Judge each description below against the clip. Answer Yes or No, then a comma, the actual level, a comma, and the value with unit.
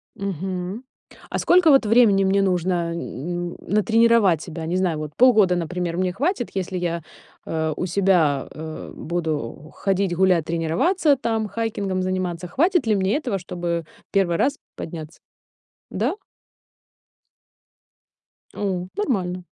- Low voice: No, medium, 185 Hz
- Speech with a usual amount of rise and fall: Yes, average, 3.7 semitones